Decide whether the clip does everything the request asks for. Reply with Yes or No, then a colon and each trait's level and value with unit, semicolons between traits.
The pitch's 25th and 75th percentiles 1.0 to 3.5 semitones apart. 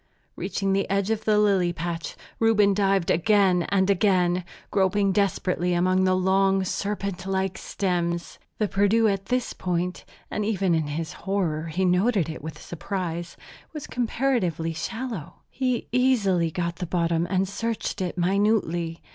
Yes: average, 2.8 semitones